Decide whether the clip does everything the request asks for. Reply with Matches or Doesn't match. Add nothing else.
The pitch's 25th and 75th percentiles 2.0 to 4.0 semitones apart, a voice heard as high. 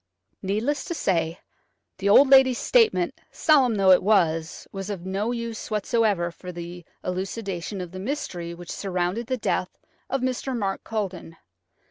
Doesn't match